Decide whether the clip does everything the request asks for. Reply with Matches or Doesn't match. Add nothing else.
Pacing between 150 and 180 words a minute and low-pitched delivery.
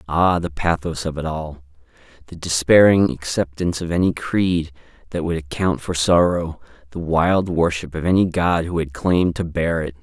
Matches